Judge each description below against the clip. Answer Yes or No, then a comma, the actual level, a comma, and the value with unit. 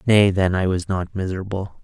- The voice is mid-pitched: No, very low, 95 Hz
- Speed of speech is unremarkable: Yes, average, 195 wpm